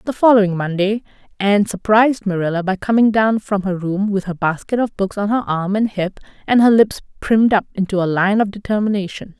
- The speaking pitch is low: No, high, 200 Hz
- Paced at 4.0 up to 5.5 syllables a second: No, 5.8 syllables/s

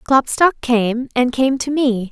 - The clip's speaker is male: No, female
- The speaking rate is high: No, average, 170 wpm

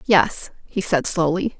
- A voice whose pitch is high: No, medium, 180 Hz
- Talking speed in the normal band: Yes, average, 150 wpm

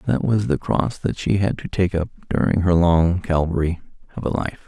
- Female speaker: No, male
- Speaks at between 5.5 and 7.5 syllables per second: No, 5.1 syllables/s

